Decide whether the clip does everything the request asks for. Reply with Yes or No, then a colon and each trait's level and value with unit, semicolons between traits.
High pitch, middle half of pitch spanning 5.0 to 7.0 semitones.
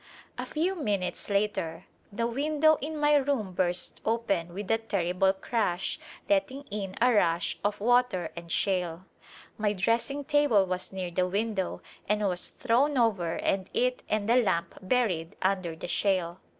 Yes: high, 205 Hz; average, 5.3 semitones